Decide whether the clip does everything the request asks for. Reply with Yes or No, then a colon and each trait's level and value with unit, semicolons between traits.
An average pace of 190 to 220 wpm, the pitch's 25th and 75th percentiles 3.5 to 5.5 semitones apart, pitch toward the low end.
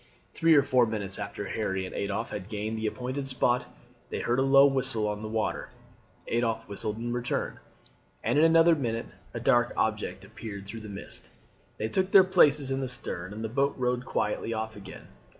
Yes: average, 195 wpm; average, 3.9 semitones; low, 115 Hz